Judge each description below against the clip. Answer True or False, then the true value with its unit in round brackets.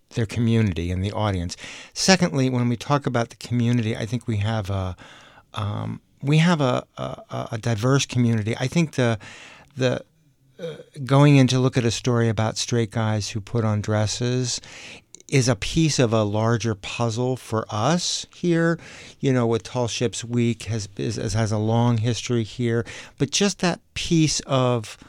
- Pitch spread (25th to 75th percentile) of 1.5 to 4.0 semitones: True (3.0 semitones)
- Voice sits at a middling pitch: False (120 Hz)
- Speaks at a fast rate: False (170 wpm)